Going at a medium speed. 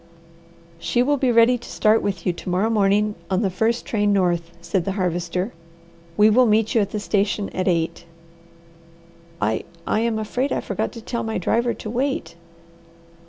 Yes: average, 180 wpm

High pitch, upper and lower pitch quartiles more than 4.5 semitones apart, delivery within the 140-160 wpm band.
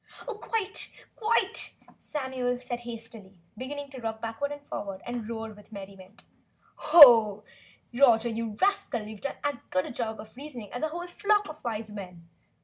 Yes: high, 240 Hz; average, 5.2 semitones; average, 150 wpm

